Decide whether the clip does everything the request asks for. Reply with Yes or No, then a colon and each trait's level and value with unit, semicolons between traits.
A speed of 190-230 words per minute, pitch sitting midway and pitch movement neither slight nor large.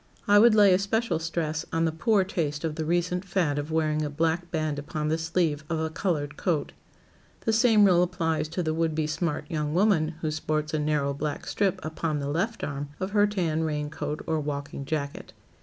Yes: fast, 205 wpm; medium, 160 Hz; average, 3.0 semitones